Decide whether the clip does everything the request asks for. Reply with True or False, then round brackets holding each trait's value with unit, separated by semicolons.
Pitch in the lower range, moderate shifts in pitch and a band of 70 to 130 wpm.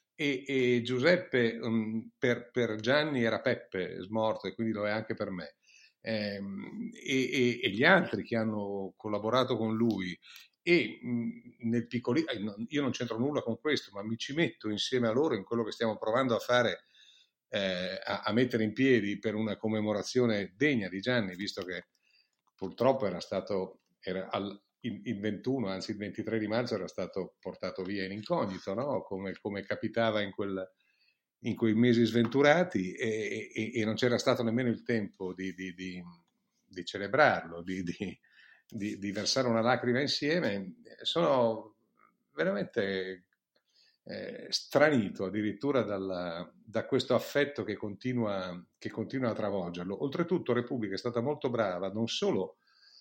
False (110 Hz; 3.4 semitones; 155 wpm)